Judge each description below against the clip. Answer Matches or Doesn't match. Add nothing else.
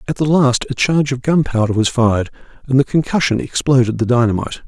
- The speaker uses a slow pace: Doesn't match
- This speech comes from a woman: Doesn't match